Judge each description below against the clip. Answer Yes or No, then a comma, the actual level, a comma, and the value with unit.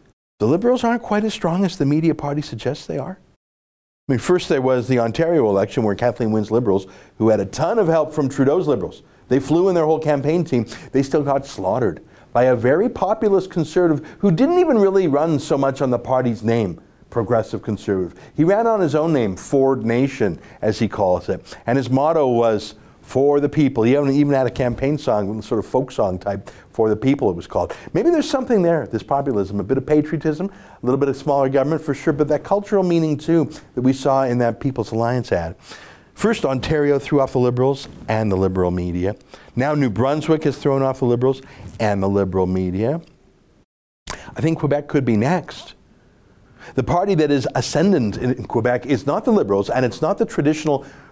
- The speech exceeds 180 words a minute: Yes, fast, 205 wpm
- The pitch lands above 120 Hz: Yes, low, 135 Hz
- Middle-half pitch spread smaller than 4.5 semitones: No, average, 5.0 semitones